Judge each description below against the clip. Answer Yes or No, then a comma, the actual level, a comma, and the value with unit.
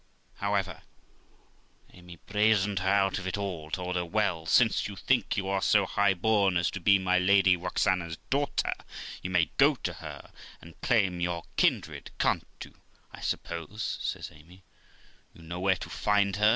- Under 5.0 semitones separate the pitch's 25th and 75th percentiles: Yes, narrow, 2.4 semitones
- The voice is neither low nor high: No, very low, 95 Hz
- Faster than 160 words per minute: Yes, average, 170 wpm